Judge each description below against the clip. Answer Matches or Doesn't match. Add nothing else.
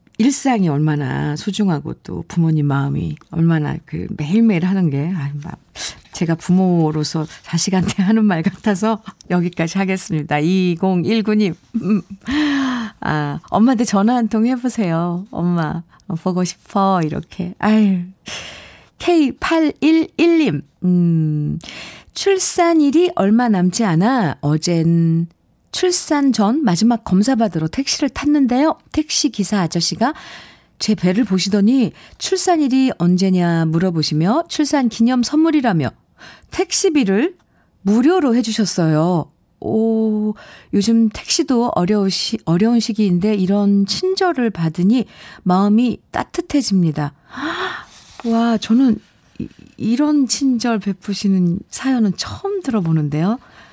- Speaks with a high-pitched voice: Matches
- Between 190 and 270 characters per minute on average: Matches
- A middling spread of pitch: Doesn't match